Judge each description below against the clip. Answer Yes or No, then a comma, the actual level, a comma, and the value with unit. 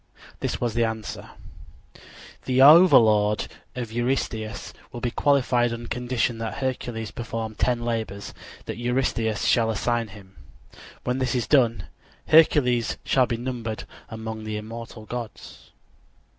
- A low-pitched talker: Yes, low, 115 Hz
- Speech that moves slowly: Yes, slow, 130 wpm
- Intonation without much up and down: Yes, narrow, 1.9 semitones